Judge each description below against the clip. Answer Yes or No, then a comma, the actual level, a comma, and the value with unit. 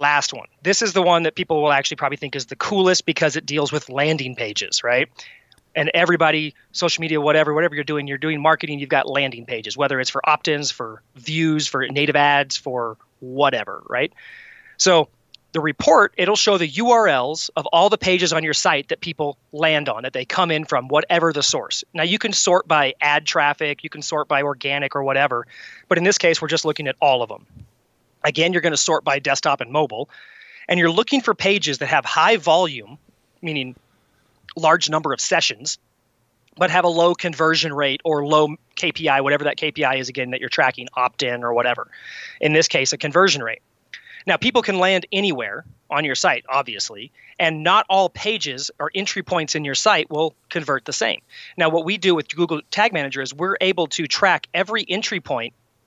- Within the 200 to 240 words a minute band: Yes, fast, 205 wpm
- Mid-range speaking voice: Yes, medium, 155 Hz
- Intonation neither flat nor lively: Yes, average, 4.2 semitones